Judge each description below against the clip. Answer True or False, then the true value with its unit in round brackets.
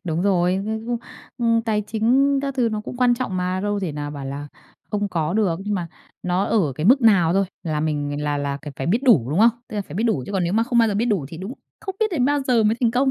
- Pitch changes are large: True (5.9 semitones)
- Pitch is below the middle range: False (205 Hz)